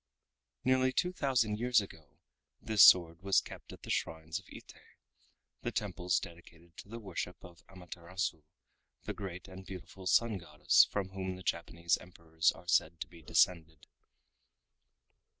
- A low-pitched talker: Yes, very low, 90 Hz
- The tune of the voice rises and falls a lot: No, average, 2.8 semitones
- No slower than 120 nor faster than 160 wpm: Yes, average, 150 wpm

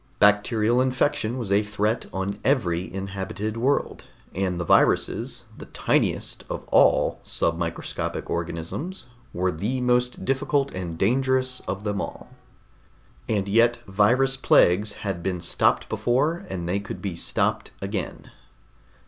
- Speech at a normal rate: No, slow, 130 wpm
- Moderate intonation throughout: Yes, average, 4.7 semitones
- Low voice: Yes, low, 105 Hz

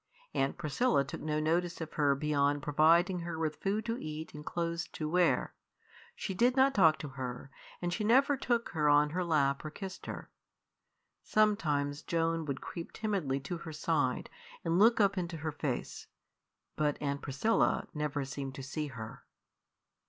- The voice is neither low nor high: Yes, medium, 155 Hz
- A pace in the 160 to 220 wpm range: Yes, average, 170 wpm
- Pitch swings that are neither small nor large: Yes, average, 3.9 semitones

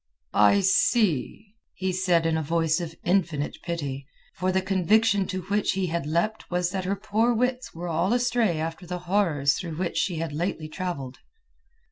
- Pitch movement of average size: Yes, average, 3.4 semitones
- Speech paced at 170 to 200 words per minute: Yes, average, 175 wpm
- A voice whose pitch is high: No, medium, 180 Hz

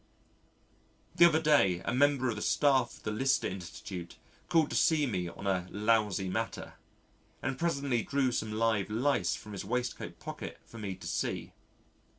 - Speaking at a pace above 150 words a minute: Yes, average, 165 wpm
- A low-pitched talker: Yes, low, 115 Hz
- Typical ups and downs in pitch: No, wide, 5.8 semitones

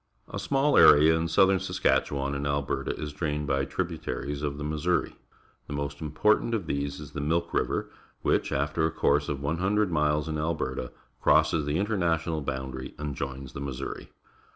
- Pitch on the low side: Yes, very low, 75 Hz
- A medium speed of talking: Yes, average, 170 wpm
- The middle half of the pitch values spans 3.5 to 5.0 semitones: No, average, 2.7 semitones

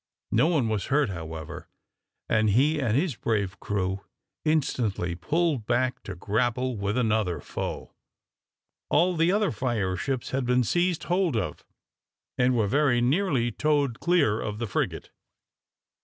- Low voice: Yes, low, 120 Hz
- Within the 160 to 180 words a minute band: No, average, 140 wpm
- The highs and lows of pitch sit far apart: Yes, wide, 6.0 semitones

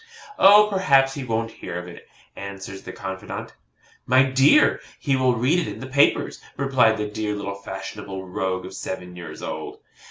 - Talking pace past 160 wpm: Yes, average, 170 wpm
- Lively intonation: Yes, wide, 5.8 semitones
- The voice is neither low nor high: No, low, 110 Hz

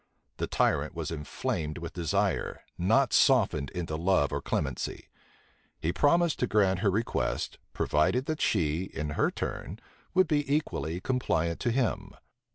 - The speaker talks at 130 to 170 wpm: Yes, average, 145 wpm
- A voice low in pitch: Yes, very low, 95 Hz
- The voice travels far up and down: Yes, wide, 8.0 semitones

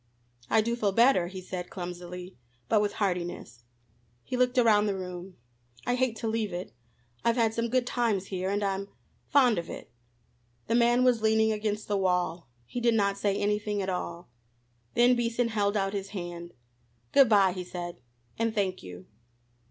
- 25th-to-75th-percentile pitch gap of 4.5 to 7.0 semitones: No, average, 4.0 semitones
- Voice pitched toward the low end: No, high, 205 Hz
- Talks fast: No, average, 175 wpm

